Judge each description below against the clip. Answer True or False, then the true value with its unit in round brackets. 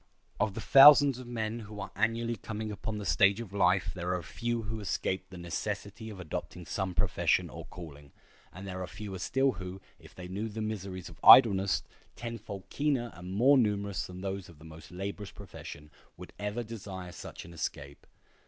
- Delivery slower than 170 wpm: False (180 wpm)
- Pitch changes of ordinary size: True (3.5 semitones)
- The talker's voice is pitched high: False (100 Hz)